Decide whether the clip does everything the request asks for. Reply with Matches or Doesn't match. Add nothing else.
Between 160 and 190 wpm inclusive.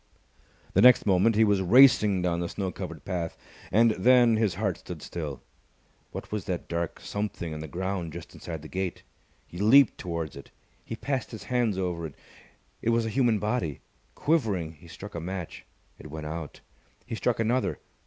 Matches